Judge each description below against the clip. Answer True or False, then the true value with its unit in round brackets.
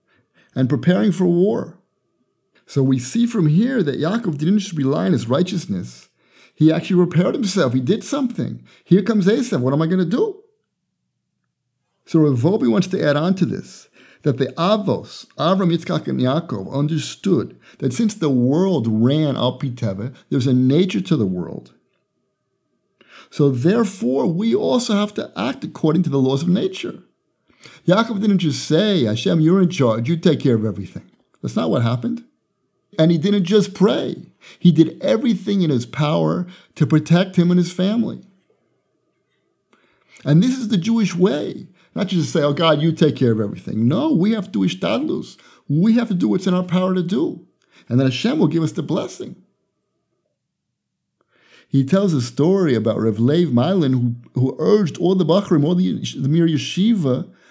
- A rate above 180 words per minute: False (175 wpm)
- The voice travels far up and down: True (5.7 semitones)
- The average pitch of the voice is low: False (170 Hz)